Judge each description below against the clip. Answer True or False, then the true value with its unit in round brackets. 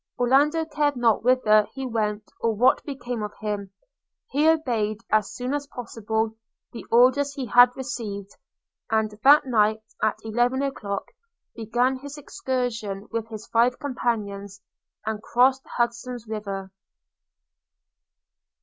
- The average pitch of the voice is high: True (235 Hz)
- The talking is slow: True (130 wpm)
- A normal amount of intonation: True (3.4 semitones)